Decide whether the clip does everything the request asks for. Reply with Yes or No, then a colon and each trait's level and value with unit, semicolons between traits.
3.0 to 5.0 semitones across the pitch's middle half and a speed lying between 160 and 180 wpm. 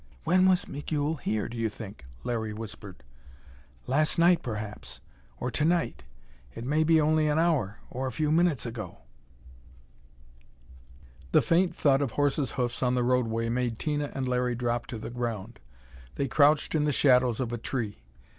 Yes: average, 4.6 semitones; average, 165 wpm